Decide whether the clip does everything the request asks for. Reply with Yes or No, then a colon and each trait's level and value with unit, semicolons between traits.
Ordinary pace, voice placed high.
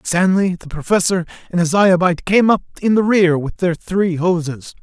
No: average, 185 wpm; medium, 180 Hz